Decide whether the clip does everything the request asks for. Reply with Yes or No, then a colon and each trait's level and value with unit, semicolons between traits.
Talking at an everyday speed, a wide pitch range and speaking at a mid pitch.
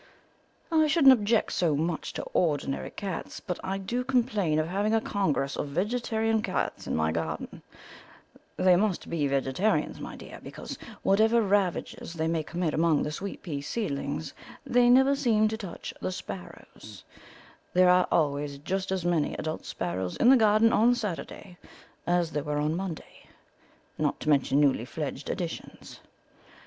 Yes: average, 155 wpm; wide, 6.4 semitones; medium, 180 Hz